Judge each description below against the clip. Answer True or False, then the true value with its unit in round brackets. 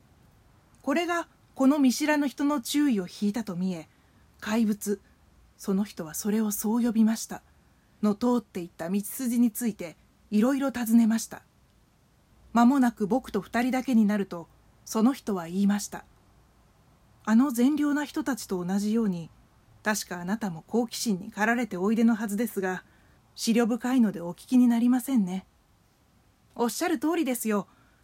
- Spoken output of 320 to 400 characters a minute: False (305 characters per minute)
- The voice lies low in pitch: False (220 Hz)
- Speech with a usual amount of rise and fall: True (3.8 semitones)